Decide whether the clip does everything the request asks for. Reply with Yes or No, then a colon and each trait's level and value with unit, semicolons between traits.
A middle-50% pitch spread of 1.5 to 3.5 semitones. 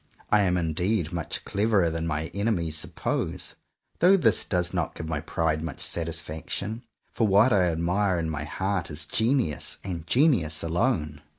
No: average, 4.4 semitones